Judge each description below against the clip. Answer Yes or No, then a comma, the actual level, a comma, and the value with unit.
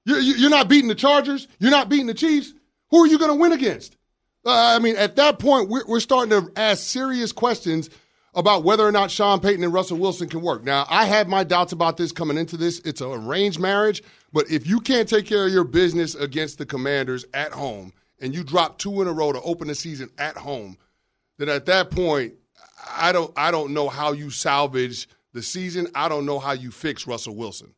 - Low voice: No, medium, 175 Hz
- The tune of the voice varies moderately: No, wide, 6.9 semitones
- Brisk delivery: Yes, fast, 220 wpm